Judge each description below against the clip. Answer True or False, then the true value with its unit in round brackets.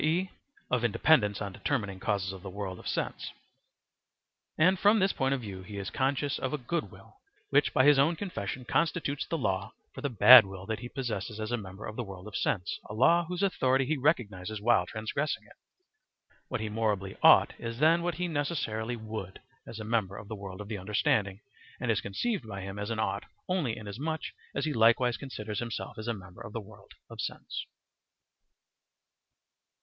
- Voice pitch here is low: True (115 Hz)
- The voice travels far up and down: True (5.8 semitones)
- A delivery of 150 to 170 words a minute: False (195 wpm)